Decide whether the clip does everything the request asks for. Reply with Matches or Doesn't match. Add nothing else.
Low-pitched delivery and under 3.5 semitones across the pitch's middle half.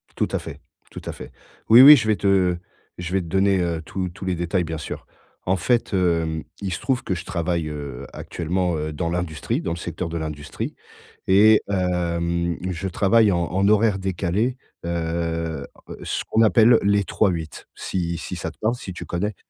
Matches